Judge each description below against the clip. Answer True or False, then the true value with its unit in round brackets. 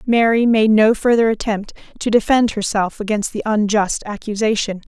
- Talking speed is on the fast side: False (145 wpm)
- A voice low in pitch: False (215 Hz)